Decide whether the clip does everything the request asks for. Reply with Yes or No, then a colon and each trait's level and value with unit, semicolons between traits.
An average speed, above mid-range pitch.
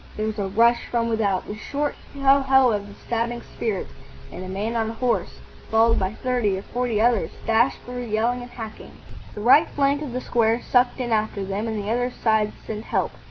No: fast, 210 wpm; high, 230 Hz